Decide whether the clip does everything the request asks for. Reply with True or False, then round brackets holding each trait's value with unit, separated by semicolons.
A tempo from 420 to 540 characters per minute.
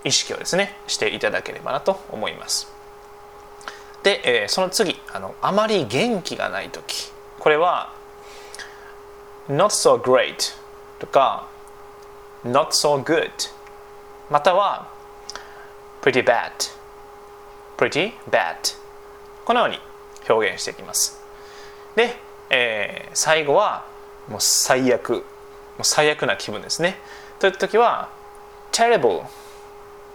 False (260 characters per minute)